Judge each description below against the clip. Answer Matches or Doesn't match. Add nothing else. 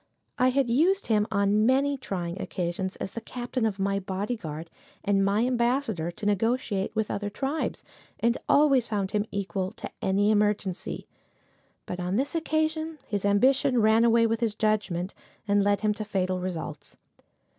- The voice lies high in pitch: Matches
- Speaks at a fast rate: Doesn't match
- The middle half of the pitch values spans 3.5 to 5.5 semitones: Matches